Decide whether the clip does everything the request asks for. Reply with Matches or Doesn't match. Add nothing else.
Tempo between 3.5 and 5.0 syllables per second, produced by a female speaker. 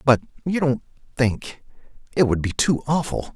Doesn't match